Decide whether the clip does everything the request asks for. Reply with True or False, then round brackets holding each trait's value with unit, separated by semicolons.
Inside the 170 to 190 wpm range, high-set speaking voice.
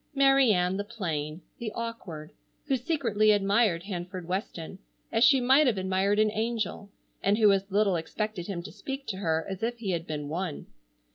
True (185 wpm; 200 Hz)